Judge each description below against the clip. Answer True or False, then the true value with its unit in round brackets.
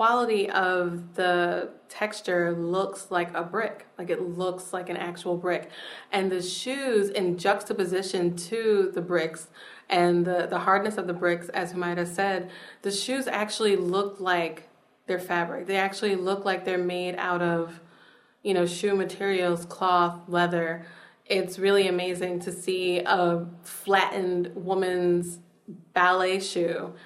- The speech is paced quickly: False (140 wpm)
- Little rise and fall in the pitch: True (1.8 semitones)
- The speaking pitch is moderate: True (180 Hz)